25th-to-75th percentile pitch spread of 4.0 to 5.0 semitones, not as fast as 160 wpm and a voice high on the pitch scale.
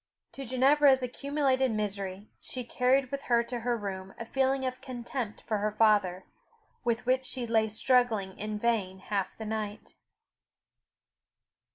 No: average, 3.6 semitones; average, 145 wpm; high, 235 Hz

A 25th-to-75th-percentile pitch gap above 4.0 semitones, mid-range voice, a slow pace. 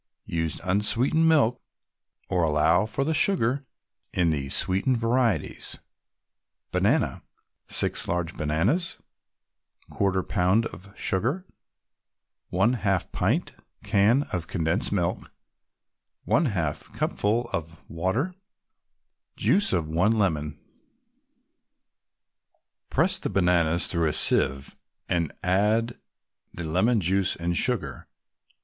No: wide, 5.6 semitones; very low, 95 Hz; slow, 100 wpm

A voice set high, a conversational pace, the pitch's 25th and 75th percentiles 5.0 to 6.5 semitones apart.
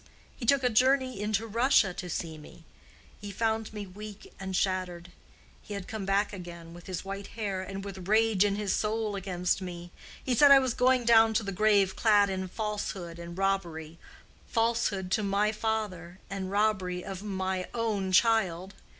No: high, 200 Hz; average, 175 wpm; average, 3.0 semitones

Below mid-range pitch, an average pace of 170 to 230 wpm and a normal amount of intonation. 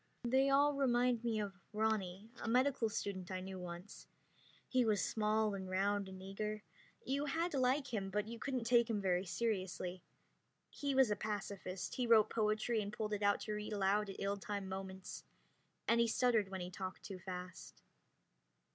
No: high, 210 Hz; average, 180 wpm; average, 3.5 semitones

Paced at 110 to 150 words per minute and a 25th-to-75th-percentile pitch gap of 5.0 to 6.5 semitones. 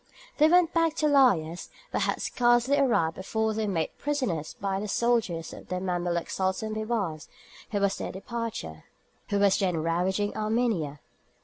Yes: average, 140 wpm; average, 5.3 semitones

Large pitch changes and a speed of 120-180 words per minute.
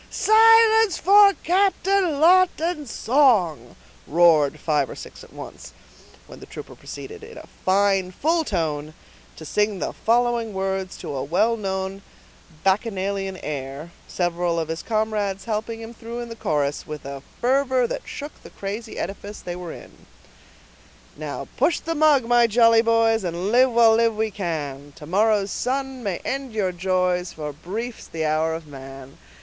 Yes: wide, 6.1 semitones; average, 155 wpm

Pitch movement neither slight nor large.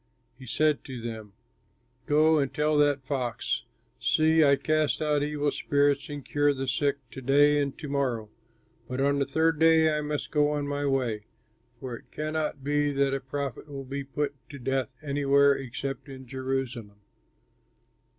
No: narrow, 1.8 semitones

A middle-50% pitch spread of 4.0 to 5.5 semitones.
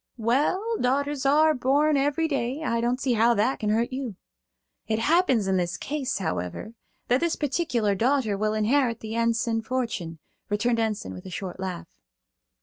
Yes: average, 4.5 semitones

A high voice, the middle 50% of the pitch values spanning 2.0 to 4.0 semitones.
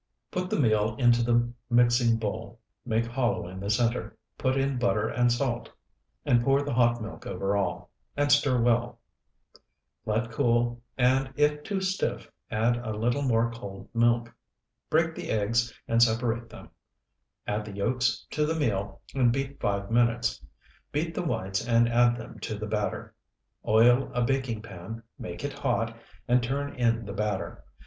No: low, 120 Hz; narrow, 2.5 semitones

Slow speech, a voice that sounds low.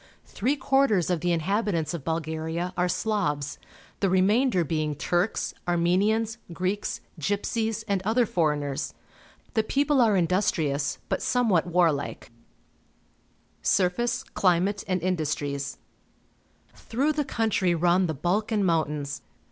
No: slow, 120 wpm; medium, 180 Hz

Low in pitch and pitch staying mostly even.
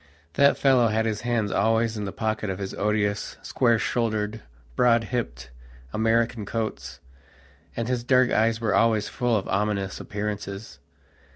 Yes: low, 110 Hz; narrow, 2.1 semitones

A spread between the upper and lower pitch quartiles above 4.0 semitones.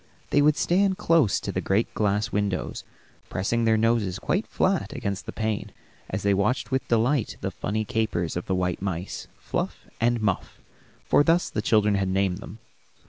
No: average, 3.7 semitones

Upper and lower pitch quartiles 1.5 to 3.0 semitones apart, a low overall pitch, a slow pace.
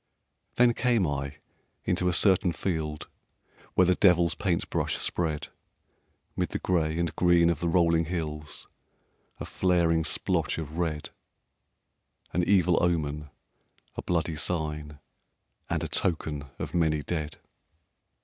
Yes: narrow, 2.5 semitones; very low, 85 Hz; slow, 130 wpm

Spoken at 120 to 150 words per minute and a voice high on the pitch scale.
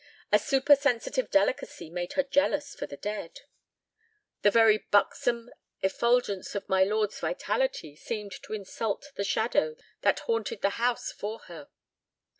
Yes: slow, 135 wpm; high, 220 Hz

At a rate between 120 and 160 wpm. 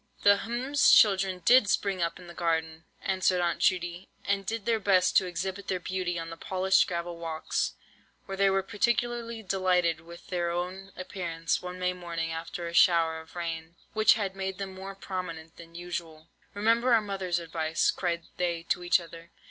No: average, 175 wpm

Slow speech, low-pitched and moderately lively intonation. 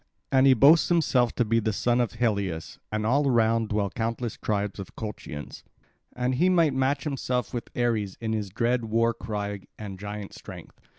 No: average, 180 wpm; low, 115 Hz; average, 3.2 semitones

